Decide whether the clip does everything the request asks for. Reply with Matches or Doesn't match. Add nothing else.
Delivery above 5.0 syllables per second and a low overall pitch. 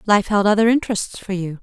Doesn't match